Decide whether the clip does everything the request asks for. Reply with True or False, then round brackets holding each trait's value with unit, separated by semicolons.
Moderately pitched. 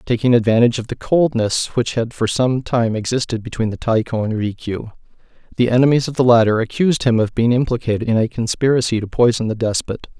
False (120 Hz)